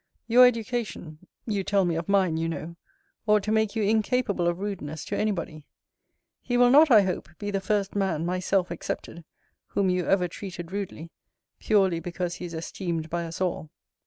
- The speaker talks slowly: No, average, 185 wpm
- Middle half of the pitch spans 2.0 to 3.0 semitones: No, average, 3.7 semitones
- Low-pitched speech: No, high, 190 Hz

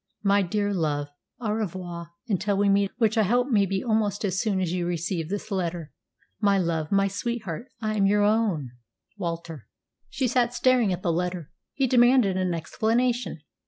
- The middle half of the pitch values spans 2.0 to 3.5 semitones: No, average, 4.1 semitones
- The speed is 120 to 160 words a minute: No, average, 175 wpm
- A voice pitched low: No, high, 195 Hz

